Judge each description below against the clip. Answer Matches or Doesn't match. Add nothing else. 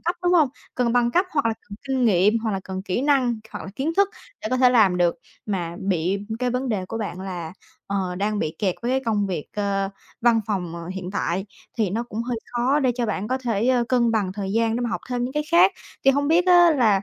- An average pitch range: Matches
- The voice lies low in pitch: Doesn't match